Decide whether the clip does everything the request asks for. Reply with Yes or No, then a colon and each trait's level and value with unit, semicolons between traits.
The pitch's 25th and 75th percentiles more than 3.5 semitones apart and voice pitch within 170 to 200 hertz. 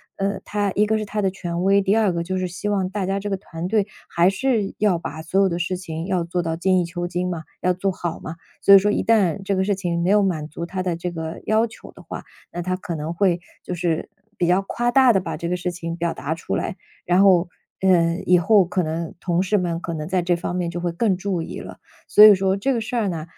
No: narrow, 2.5 semitones; medium, 185 Hz